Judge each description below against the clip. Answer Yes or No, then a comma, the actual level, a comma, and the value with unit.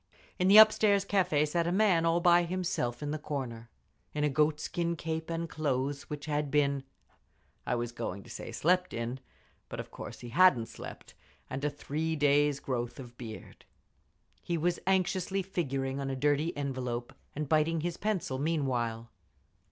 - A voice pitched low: No, medium, 150 Hz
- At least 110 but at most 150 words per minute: No, average, 165 wpm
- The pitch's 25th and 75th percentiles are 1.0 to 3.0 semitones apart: No, average, 4.3 semitones